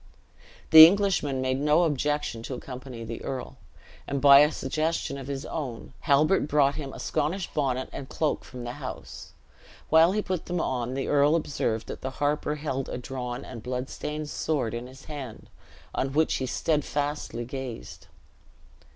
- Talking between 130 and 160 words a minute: No, average, 170 wpm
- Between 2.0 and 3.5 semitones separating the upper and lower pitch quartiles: Yes, average, 2.8 semitones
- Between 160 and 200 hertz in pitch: No, medium, 140 Hz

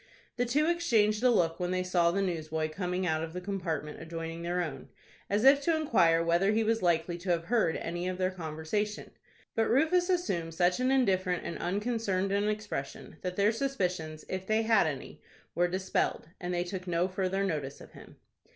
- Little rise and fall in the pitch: No, average, 4.1 semitones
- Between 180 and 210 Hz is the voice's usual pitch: Yes, medium, 185 Hz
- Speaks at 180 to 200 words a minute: Yes, average, 195 wpm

